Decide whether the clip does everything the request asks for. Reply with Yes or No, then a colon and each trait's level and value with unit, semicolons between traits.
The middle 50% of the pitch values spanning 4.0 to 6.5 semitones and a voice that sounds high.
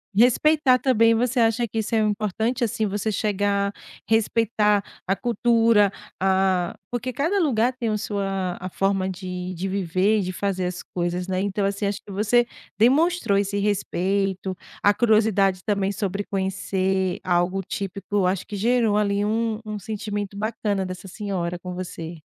No: average, 2.7 semitones; high, 200 Hz